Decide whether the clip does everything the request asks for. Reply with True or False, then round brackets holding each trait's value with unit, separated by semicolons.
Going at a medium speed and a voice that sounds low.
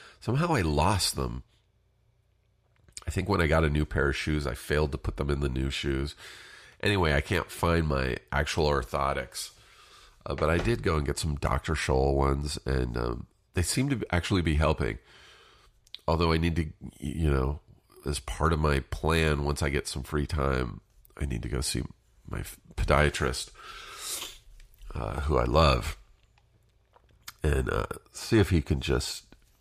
True (170 wpm; 75 Hz)